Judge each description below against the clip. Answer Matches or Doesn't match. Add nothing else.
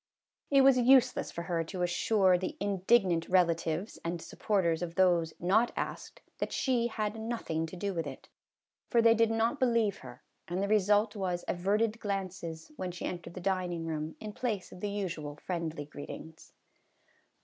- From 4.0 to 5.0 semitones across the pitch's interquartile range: Matches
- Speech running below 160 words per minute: Doesn't match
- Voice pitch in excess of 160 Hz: Matches